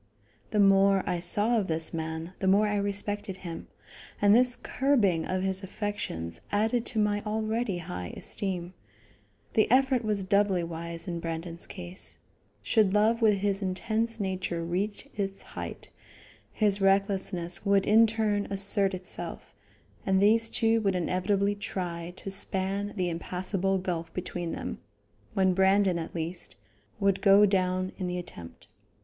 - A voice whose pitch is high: Yes, high, 195 Hz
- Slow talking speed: No, average, 145 wpm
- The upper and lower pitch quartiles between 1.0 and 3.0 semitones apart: Yes, narrow, 2.5 semitones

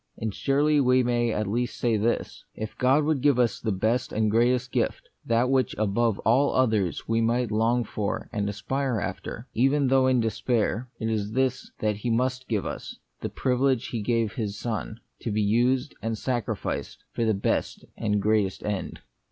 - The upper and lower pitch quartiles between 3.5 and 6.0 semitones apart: No, average, 2.9 semitones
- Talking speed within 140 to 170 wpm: No, average, 185 wpm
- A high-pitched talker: No, low, 115 Hz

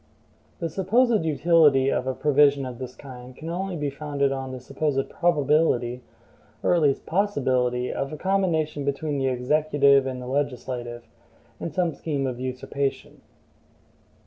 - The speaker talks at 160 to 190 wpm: No, average, 145 wpm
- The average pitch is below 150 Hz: Yes, medium, 140 Hz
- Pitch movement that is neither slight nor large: Yes, average, 3.5 semitones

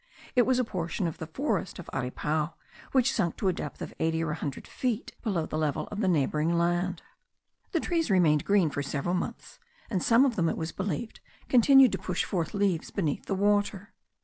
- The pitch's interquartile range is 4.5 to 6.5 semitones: Yes, average, 5.1 semitones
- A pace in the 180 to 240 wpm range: Yes, fast, 205 wpm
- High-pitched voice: No, medium, 180 Hz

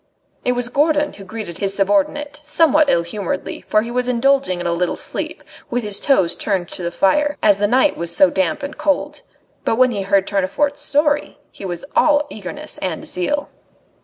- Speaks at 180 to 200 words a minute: Yes, average, 190 wpm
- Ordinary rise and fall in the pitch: No, wide, 7.3 semitones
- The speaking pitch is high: Yes, high, 225 Hz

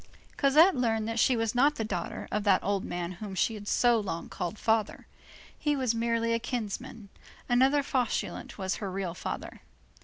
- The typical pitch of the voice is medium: No, high, 225 Hz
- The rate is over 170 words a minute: Yes, average, 180 wpm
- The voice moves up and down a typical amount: Yes, average, 3.4 semitones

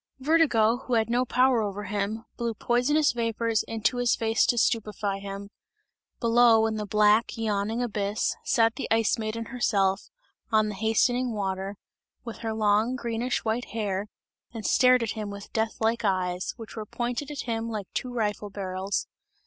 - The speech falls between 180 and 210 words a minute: No, average, 165 wpm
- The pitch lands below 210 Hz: No, high, 225 Hz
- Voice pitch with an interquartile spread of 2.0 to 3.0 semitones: Yes, narrow, 2.4 semitones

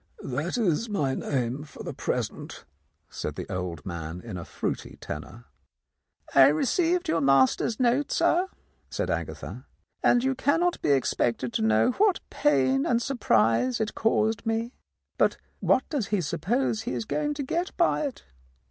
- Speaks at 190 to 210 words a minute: No, average, 155 wpm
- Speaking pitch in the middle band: No, high, 210 Hz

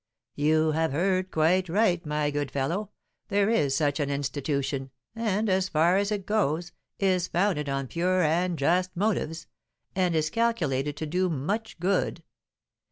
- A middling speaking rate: Yes, average, 155 wpm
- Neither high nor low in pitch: Yes, medium, 170 Hz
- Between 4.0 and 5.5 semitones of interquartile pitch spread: Yes, average, 4.3 semitones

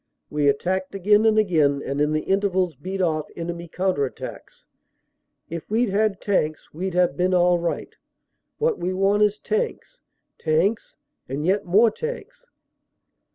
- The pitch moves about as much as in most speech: Yes, average, 3.9 semitones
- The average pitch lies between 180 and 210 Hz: Yes, medium, 185 Hz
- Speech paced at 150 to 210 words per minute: Yes, average, 155 wpm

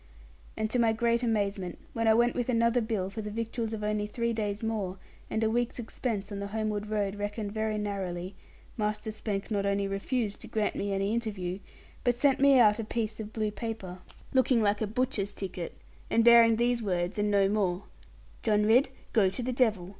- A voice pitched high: Yes, high, 215 Hz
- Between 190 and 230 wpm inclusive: Yes, average, 200 wpm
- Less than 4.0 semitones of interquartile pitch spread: Yes, narrow, 2.4 semitones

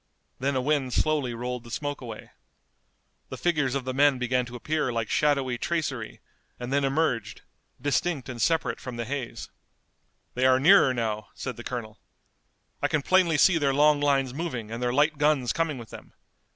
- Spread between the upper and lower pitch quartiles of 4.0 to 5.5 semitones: No, average, 3.4 semitones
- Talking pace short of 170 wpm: No, average, 180 wpm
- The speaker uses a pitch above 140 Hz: No, low, 135 Hz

